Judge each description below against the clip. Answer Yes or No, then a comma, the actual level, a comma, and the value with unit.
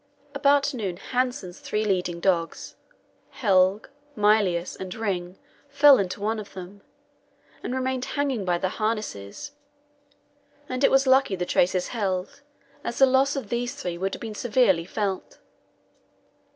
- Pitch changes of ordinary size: No, wide, 5.8 semitones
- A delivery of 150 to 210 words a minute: No, average, 140 wpm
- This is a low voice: No, high, 210 Hz